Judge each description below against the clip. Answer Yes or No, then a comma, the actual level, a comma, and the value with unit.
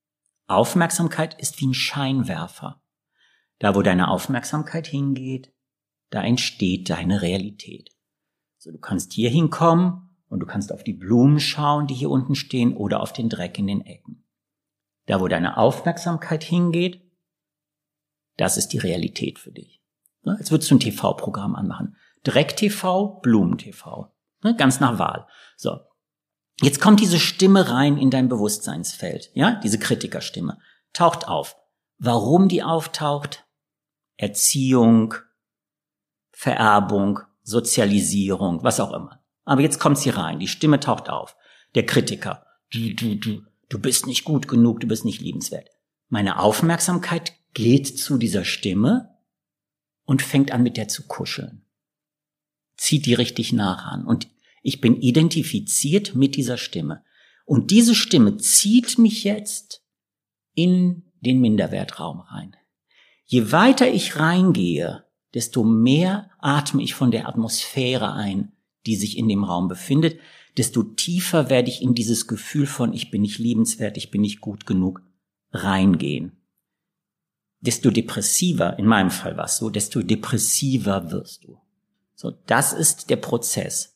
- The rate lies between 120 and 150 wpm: Yes, average, 135 wpm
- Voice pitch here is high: No, low, 135 Hz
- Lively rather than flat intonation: Yes, wide, 6.0 semitones